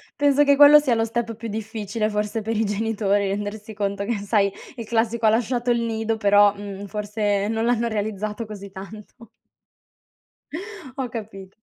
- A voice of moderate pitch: No, high, 220 Hz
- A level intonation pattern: Yes, narrow, 2.1 semitones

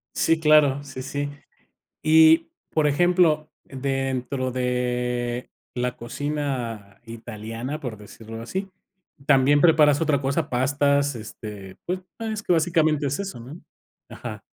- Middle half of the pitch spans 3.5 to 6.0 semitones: Yes, average, 3.9 semitones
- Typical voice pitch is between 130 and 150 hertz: Yes, medium, 140 Hz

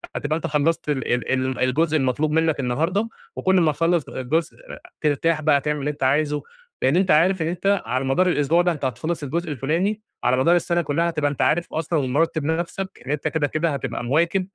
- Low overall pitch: No, medium, 155 Hz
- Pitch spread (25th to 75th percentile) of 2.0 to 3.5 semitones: Yes, average, 3.2 semitones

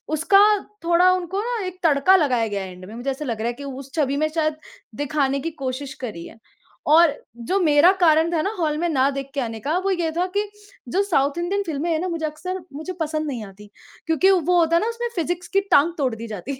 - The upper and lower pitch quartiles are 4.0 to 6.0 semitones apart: Yes, average, 4.3 semitones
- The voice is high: Yes, very high, 310 Hz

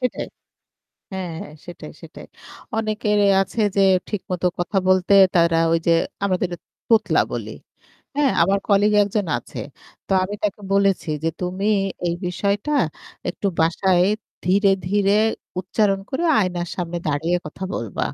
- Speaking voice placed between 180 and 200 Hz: Yes, high, 190 Hz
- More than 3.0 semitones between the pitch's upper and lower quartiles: No, average, 2.7 semitones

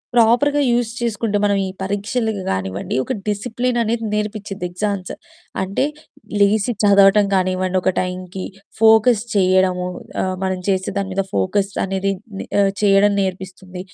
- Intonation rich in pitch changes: No, narrow, 2.4 semitones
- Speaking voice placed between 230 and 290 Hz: No, high, 200 Hz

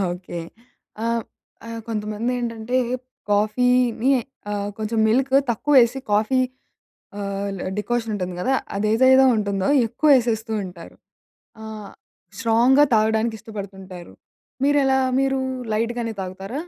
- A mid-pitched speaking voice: No, high, 225 Hz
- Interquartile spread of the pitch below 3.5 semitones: Yes, average, 3.1 semitones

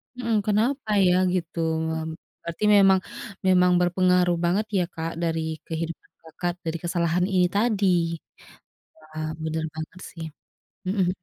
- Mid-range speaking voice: Yes, medium, 175 Hz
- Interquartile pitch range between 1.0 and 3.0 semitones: Yes, average, 2.7 semitones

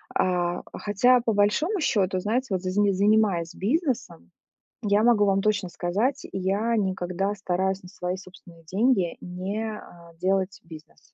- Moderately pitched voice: No, high, 195 Hz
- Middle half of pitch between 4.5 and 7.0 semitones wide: No, average, 2.9 semitones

